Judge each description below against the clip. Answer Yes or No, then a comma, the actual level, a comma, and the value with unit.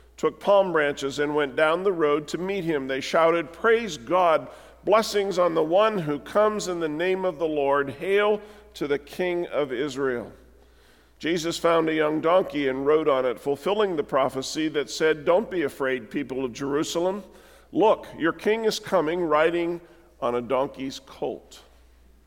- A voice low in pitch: No, medium, 160 Hz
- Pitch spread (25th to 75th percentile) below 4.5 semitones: No, average, 4.8 semitones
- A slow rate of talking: No, average, 170 wpm